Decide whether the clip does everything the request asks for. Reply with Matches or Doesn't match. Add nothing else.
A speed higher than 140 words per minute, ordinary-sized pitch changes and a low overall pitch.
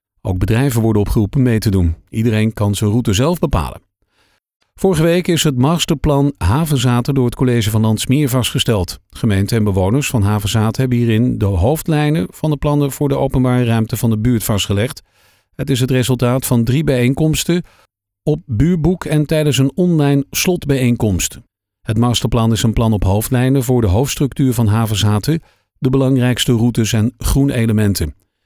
Matches